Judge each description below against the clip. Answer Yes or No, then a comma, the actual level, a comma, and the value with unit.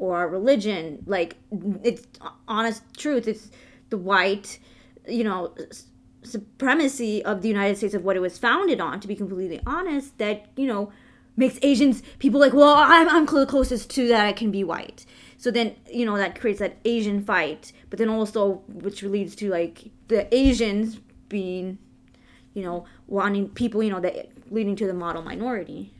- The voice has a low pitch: No, high, 215 Hz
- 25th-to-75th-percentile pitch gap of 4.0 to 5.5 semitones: No, average, 3.6 semitones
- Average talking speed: Yes, average, 170 wpm